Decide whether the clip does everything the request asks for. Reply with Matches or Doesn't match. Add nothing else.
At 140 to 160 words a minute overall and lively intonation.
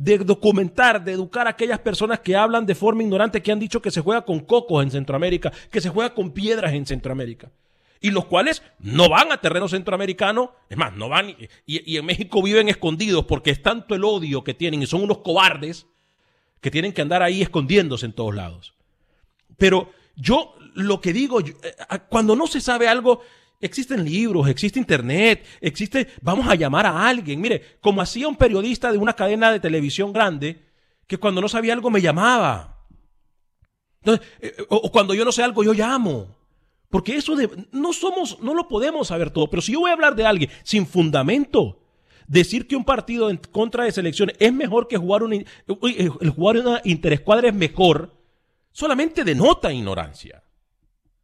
Doesn't match